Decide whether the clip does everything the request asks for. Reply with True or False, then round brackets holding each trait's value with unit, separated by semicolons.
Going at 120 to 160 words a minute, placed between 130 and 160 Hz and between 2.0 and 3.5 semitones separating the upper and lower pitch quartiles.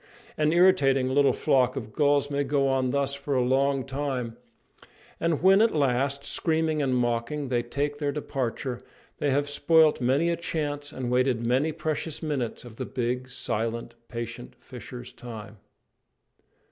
True (155 wpm; 135 Hz; 2.9 semitones)